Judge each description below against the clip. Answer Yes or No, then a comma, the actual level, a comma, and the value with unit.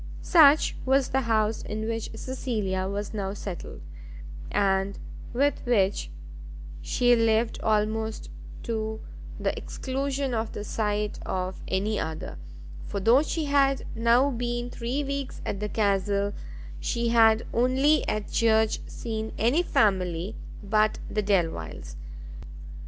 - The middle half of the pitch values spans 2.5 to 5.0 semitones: Yes, average, 3.3 semitones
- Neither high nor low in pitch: No, high, 220 Hz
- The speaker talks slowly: Yes, slow, 125 wpm